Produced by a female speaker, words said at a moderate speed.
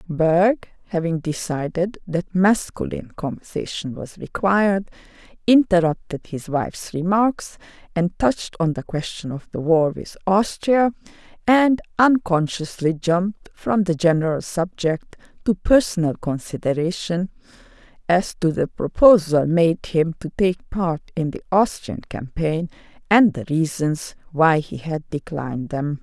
No: female; slow, 120 wpm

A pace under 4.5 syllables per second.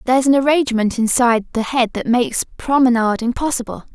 No: 6.5 syllables/s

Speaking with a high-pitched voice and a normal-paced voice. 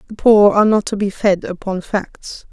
No: high, 200 Hz; fast, 215 wpm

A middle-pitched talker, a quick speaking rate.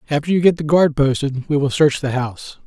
Yes: medium, 145 Hz; fast, 245 wpm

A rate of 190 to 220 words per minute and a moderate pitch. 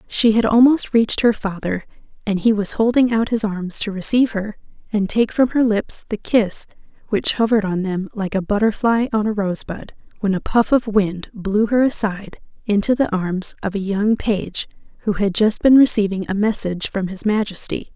No: average, 195 wpm; high, 210 Hz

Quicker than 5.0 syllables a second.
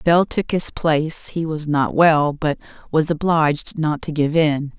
No: 4.2 syllables/s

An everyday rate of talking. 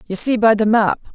No: fast, 265 wpm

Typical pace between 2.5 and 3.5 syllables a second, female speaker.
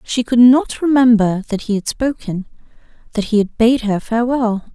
No: 5.0 syllables/s; female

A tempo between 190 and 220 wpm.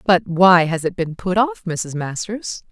Yes: average, 200 wpm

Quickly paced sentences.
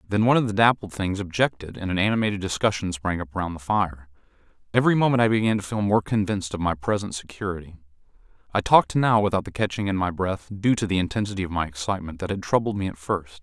Yes: fast, 225 wpm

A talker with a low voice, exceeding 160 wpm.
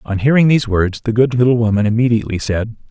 Yes: low, 115 Hz; fast, 205 wpm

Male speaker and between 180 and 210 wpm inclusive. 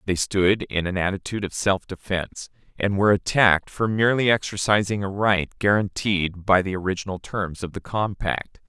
No: male; average, 165 wpm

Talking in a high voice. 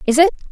Yes: very high, 295 Hz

